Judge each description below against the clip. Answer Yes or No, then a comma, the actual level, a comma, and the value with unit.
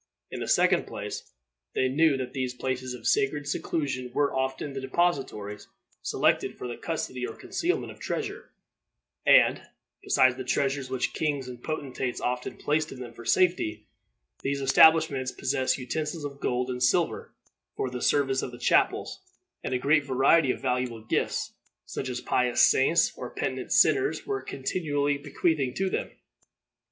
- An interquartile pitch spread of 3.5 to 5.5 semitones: No, narrow, 2.6 semitones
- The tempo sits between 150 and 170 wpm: Yes, average, 160 wpm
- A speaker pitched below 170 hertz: Yes, low, 135 Hz